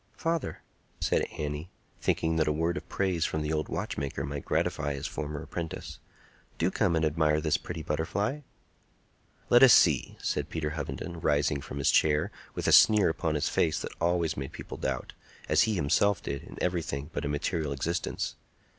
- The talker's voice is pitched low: Yes, very low, 80 Hz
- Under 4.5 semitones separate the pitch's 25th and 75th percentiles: Yes, average, 2.7 semitones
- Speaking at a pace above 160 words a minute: Yes, average, 180 wpm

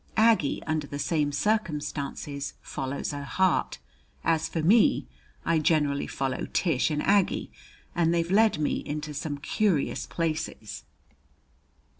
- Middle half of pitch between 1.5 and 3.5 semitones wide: Yes, average, 3.2 semitones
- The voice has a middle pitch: Yes, medium, 155 Hz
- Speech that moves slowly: Yes, slow, 125 wpm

